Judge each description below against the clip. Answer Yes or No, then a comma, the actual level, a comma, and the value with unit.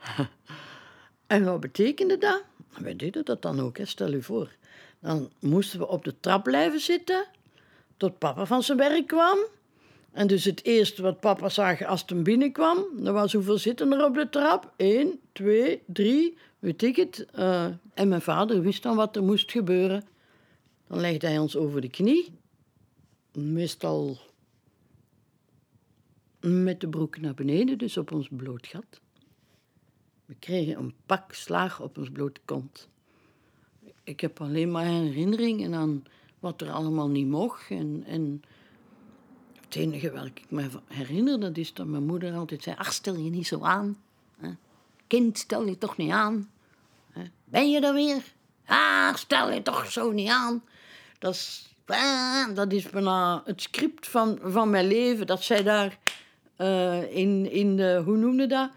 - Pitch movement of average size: No, wide, 6.5 semitones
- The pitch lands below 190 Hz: No, high, 195 Hz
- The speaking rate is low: No, average, 160 wpm